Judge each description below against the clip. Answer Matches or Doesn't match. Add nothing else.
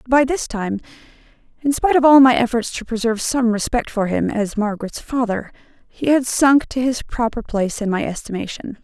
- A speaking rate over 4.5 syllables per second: Doesn't match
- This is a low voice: Doesn't match